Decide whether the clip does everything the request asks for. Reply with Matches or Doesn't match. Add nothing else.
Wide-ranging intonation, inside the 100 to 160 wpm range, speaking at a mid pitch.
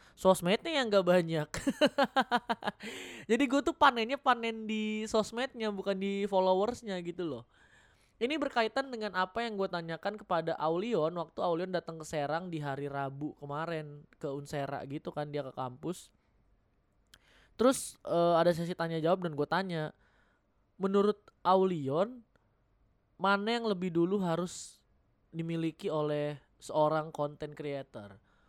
Matches